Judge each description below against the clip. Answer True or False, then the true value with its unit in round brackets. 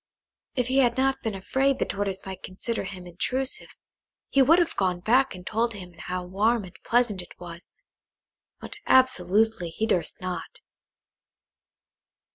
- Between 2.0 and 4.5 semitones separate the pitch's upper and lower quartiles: False (5.6 semitones)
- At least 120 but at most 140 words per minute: False (150 wpm)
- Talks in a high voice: True (205 Hz)